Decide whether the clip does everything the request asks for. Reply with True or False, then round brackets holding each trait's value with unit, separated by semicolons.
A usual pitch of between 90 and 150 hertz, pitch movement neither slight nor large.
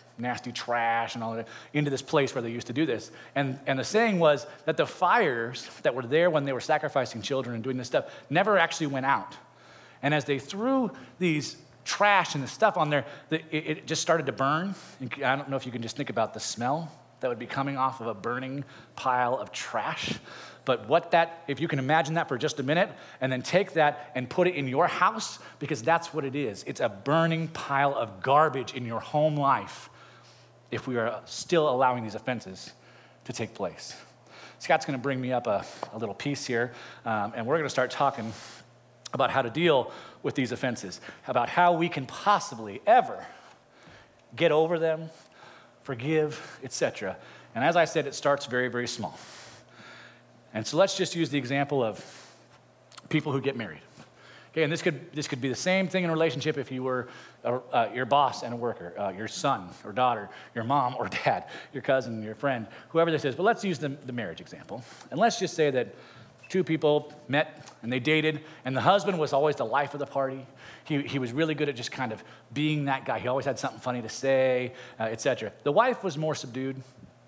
True (140 Hz; 3.9 semitones)